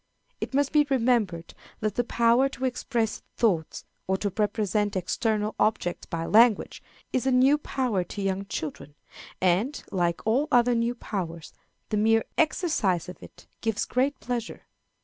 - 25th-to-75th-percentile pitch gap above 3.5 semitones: Yes, average, 4.7 semitones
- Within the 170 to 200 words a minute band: No, average, 150 wpm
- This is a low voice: No, high, 220 Hz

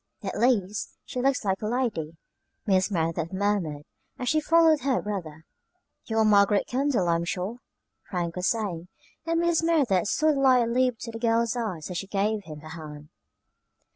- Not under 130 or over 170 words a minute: No, average, 180 wpm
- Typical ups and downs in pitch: No, wide, 6.1 semitones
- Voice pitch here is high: Yes, high, 210 Hz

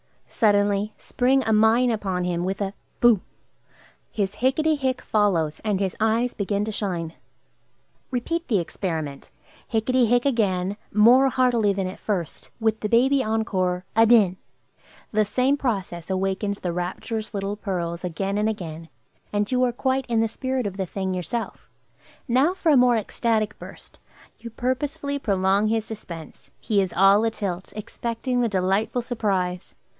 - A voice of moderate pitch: No, high, 210 Hz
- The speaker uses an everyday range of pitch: Yes, average, 4.1 semitones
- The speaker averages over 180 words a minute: No, average, 150 wpm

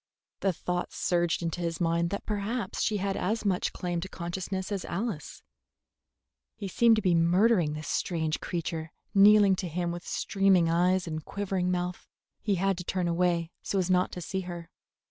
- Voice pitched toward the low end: No, medium, 180 Hz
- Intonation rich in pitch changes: No, narrow, 2.4 semitones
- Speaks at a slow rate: No, average, 180 wpm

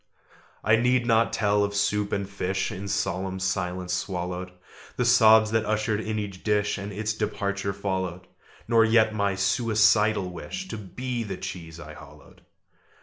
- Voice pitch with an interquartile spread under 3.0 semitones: Yes, narrow, 2.6 semitones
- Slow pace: No, average, 155 wpm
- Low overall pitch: Yes, low, 100 Hz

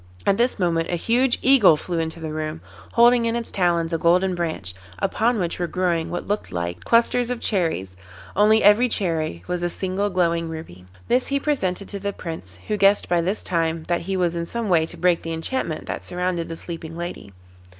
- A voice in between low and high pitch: Yes, medium, 175 Hz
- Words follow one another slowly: No, fast, 205 wpm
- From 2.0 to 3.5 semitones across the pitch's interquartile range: No, average, 3.9 semitones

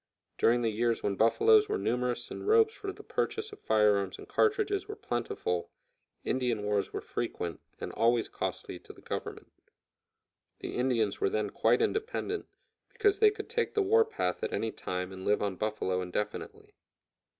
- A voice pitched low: Yes, low, 120 Hz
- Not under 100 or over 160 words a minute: No, average, 170 wpm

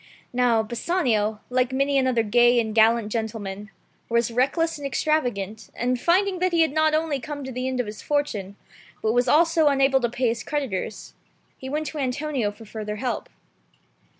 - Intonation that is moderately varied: Yes, average, 4.7 semitones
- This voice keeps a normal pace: Yes, average, 180 wpm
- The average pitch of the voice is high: Yes, very high, 250 Hz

